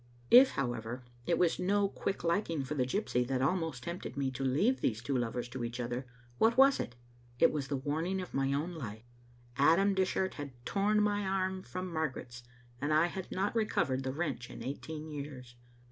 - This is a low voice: No, medium, 150 Hz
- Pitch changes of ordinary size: No, wide, 6.5 semitones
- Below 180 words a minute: No, average, 190 wpm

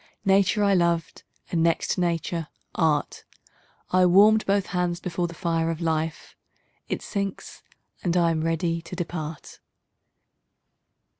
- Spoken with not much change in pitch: Yes, narrow, 1.9 semitones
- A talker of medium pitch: Yes, medium, 170 Hz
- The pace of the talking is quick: No, slow, 135 wpm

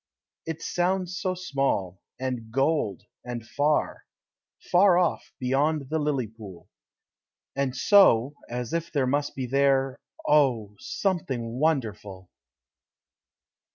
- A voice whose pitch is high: No, low, 135 Hz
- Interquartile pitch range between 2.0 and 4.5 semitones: No, average, 5.1 semitones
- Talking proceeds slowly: Yes, slow, 110 wpm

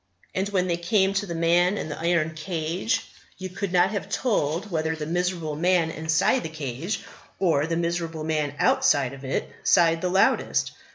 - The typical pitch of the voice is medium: Yes, medium, 170 Hz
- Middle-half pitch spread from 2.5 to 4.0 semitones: Yes, average, 2.8 semitones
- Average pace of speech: Yes, average, 180 wpm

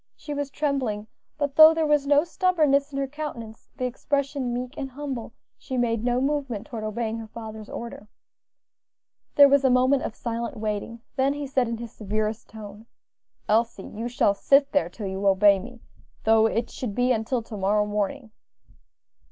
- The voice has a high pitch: Yes, high, 240 Hz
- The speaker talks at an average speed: Yes, average, 175 wpm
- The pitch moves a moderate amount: Yes, average, 4.3 semitones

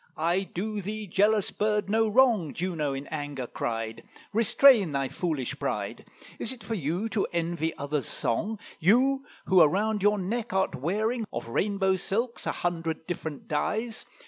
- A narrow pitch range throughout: No, wide, 5.6 semitones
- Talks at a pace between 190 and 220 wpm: No, average, 155 wpm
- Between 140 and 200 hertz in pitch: Yes, high, 190 Hz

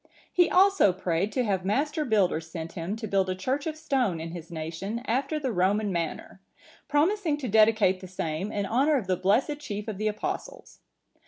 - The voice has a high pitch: Yes, high, 210 Hz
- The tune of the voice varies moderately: No, wide, 6.8 semitones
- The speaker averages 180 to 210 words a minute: Yes, average, 190 wpm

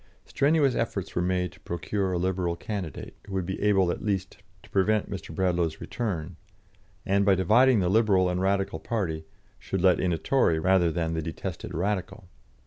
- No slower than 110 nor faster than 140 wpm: No, average, 180 wpm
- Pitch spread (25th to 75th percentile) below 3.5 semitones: Yes, average, 2.8 semitones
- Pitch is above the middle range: No, very low, 95 Hz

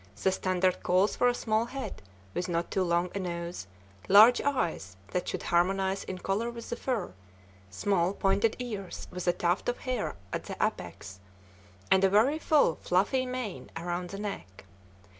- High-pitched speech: Yes, high, 195 Hz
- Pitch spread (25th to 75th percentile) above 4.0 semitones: Yes, average, 4.5 semitones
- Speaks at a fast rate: No, average, 170 wpm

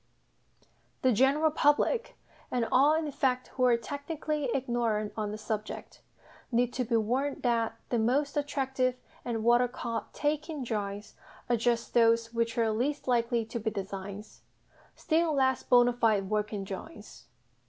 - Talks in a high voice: Yes, high, 240 Hz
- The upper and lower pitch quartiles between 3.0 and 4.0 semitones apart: Yes, average, 3.6 semitones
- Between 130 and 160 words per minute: Yes, average, 150 wpm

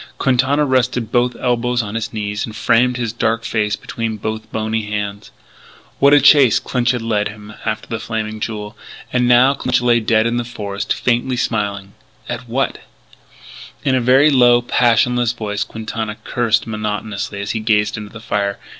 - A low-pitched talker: Yes, low, 115 Hz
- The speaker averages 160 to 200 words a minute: Yes, average, 170 wpm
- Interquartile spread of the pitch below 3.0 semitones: Yes, narrow, 2.4 semitones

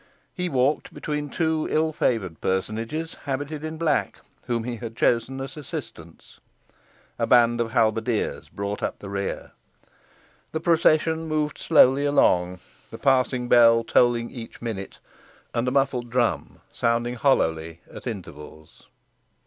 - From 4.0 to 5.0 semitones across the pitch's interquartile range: Yes, average, 4.6 semitones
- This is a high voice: No, low, 120 Hz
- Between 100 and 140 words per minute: Yes, slow, 135 wpm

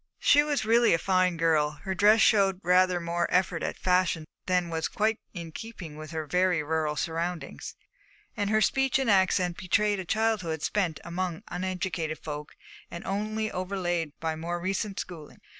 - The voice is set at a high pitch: No, medium, 180 Hz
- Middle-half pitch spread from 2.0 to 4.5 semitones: Yes, average, 3.5 semitones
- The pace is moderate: Yes, average, 165 wpm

